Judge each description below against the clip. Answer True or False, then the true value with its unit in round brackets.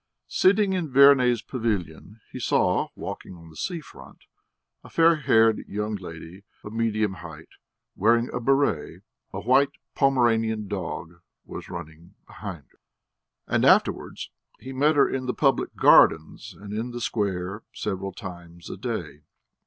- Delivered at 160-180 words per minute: False (145 wpm)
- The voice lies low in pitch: True (110 Hz)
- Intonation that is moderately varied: False (6.3 semitones)